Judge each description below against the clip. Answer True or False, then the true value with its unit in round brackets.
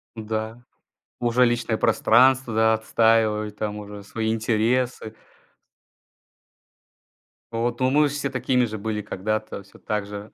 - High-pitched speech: False (110 Hz)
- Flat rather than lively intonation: True (2.2 semitones)